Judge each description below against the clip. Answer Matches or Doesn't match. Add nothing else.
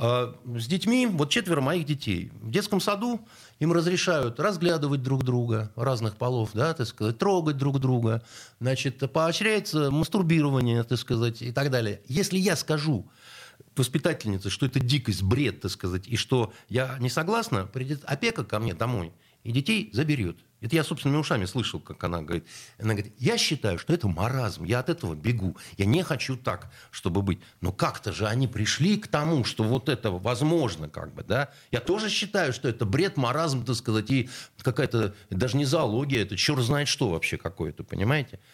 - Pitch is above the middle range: Doesn't match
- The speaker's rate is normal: Doesn't match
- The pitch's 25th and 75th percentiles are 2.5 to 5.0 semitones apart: Doesn't match